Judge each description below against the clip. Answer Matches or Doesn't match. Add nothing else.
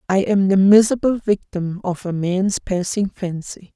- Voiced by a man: Doesn't match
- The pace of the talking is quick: Doesn't match